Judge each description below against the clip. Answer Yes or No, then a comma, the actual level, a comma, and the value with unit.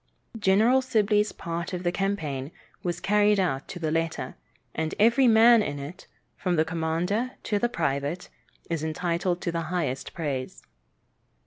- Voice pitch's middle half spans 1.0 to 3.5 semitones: No, average, 4.5 semitones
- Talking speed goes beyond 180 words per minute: No, average, 150 wpm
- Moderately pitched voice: Yes, medium, 175 Hz